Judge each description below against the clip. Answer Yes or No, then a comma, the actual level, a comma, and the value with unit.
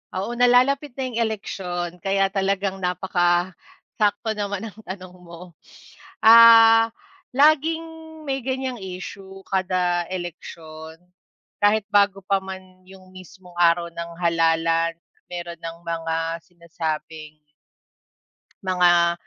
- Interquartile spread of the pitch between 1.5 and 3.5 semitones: Yes, average, 3.2 semitones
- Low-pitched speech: No, medium, 185 Hz